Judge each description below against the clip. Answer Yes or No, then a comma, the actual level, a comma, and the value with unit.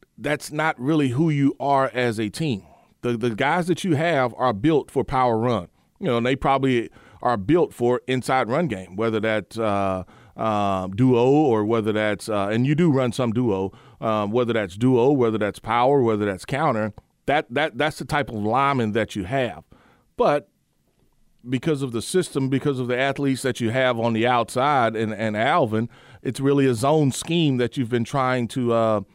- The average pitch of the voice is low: Yes, low, 125 Hz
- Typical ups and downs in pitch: Yes, average, 3.8 semitones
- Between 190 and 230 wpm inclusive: Yes, average, 195 wpm